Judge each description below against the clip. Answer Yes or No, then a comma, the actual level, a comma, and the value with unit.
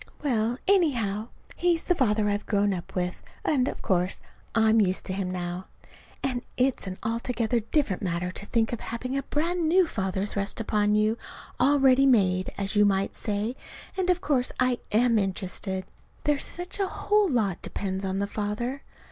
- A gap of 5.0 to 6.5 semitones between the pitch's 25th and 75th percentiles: Yes, average, 5.3 semitones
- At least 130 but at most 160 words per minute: No, average, 175 wpm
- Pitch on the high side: Yes, high, 220 Hz